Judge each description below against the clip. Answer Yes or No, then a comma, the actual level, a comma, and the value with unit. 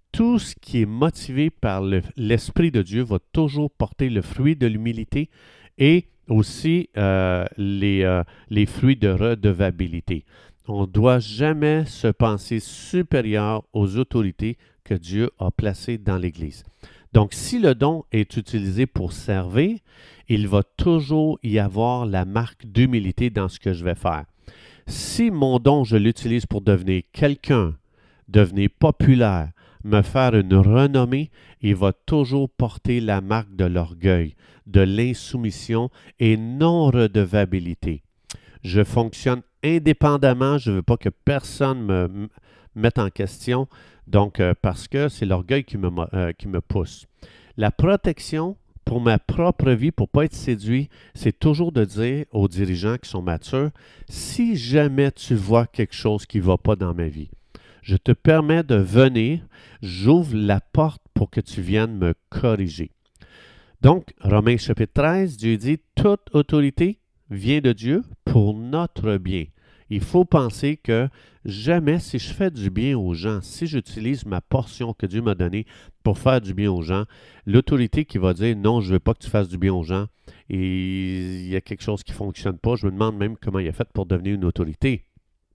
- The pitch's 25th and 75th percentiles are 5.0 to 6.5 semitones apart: Yes, average, 5.3 semitones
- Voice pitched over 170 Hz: No, low, 110 Hz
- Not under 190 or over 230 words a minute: No, average, 170 wpm